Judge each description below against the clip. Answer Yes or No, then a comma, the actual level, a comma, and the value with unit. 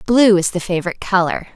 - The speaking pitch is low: No, high, 190 Hz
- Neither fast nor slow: Yes, average, 195 wpm